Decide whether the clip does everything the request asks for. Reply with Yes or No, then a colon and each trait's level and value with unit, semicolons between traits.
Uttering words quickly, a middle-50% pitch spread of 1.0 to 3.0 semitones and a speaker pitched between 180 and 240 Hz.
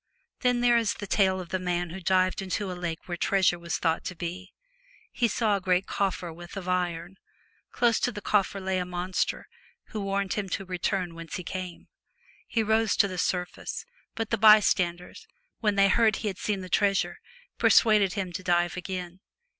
Yes: fast, 210 wpm; narrow, 2.4 semitones; medium, 185 Hz